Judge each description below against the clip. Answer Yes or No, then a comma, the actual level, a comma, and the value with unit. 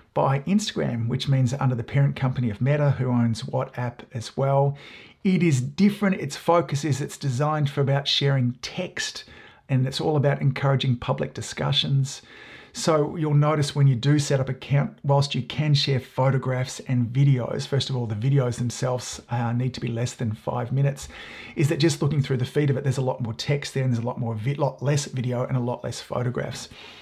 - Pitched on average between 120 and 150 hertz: Yes, low, 135 Hz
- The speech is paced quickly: Yes, fast, 210 wpm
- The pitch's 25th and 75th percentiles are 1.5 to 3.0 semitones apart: Yes, narrow, 2.4 semitones